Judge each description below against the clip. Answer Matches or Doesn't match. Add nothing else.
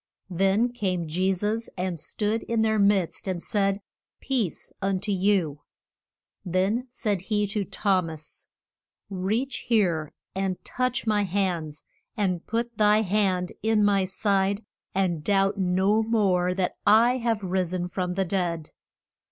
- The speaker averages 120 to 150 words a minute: Matches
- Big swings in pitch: Doesn't match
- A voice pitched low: Doesn't match